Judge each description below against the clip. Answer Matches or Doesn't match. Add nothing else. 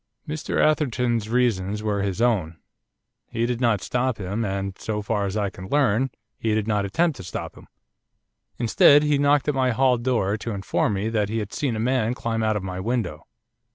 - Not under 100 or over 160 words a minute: Doesn't match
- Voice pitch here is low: Matches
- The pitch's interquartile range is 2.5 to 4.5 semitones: Matches